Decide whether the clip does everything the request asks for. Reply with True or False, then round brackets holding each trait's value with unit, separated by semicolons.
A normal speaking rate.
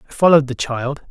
False (215 wpm)